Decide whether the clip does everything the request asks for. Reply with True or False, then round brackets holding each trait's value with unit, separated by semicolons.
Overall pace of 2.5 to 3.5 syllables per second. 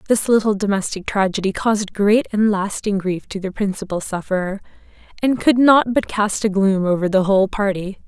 False (5.3 syllables/s)